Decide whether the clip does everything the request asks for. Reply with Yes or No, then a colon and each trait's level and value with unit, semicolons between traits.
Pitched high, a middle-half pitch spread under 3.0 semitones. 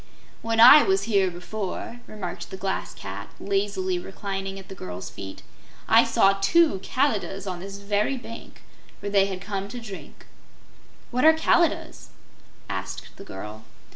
Yes: high, 195 Hz; narrow, 2.4 semitones